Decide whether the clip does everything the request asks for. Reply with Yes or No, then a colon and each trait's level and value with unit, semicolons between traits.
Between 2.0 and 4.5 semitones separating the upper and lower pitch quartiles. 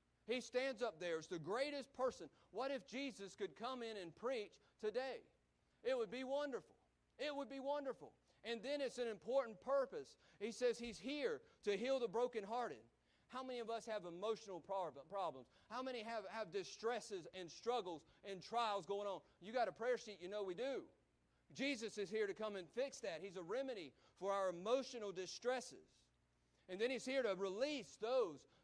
No: average, 4.9 semitones